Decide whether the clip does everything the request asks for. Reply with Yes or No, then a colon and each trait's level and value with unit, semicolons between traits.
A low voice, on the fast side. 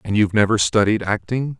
No: low, 105 Hz; average, 190 wpm